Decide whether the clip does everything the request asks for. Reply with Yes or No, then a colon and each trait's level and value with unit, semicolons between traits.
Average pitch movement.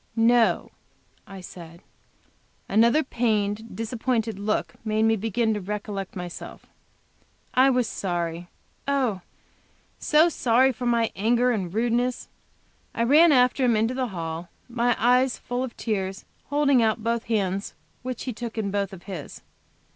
Yes: average, 3.6 semitones